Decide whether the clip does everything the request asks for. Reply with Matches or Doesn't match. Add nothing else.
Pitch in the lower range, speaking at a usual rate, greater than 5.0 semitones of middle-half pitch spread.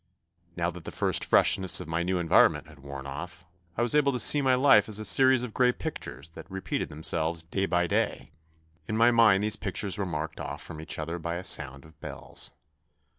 Doesn't match